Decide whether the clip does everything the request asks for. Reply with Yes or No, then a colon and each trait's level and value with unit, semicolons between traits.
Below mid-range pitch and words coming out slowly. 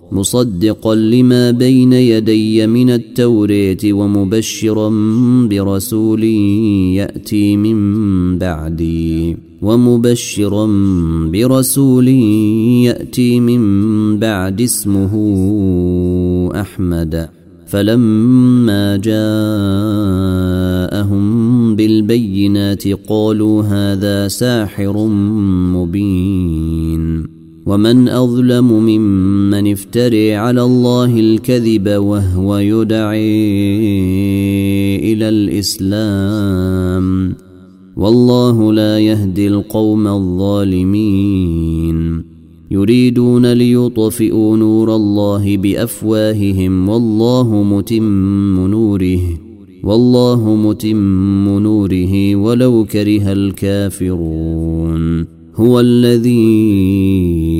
Yes: low, 105 Hz; slow, 60 wpm